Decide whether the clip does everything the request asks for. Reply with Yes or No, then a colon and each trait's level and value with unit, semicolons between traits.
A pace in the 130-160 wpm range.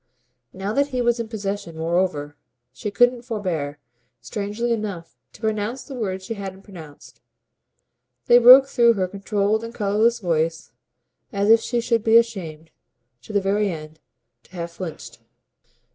Yes: average, 150 wpm